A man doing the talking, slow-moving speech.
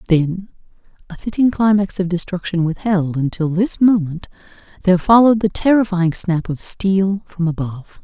No: female; slow, 125 wpm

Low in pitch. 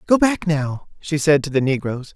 No: medium, 155 Hz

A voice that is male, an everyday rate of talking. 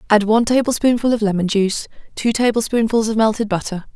No: female; average, 165 wpm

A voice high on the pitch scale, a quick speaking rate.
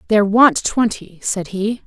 No: high, 210 Hz; average, 160 wpm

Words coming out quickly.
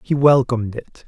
No: average, 170 wpm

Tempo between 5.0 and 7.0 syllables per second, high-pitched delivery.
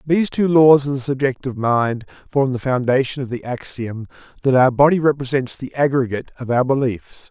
No: 5.5 syllables/s; low, 130 Hz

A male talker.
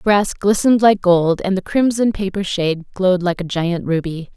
No: female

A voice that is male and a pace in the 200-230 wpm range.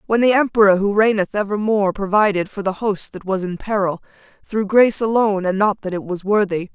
No: female; fast, 205 wpm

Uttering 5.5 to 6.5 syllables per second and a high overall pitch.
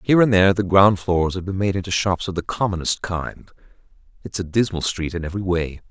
No: 6.0 syllables/s; very low, 95 Hz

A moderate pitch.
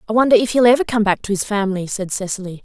No: high, 210 Hz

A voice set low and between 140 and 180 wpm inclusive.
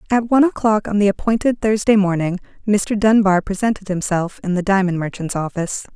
No: high, 200 Hz; average, 170 wpm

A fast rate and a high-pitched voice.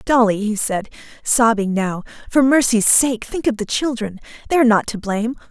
No: average, 185 wpm; high, 230 Hz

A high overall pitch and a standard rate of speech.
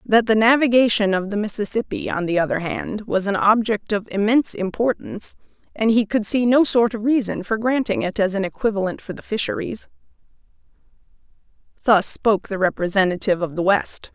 Yes: high, 210 Hz; average, 170 wpm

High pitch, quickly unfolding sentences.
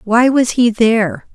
No: high, 225 Hz; average, 180 wpm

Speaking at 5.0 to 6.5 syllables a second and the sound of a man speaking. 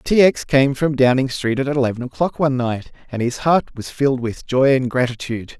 Yes: 5.5 syllables/s; male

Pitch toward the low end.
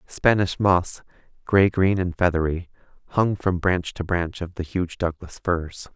Yes: very low, 90 Hz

